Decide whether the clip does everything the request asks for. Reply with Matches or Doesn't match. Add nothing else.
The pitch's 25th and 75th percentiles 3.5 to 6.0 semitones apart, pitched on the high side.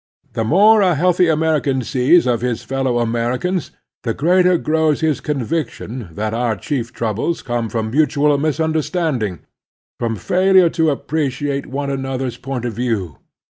Doesn't match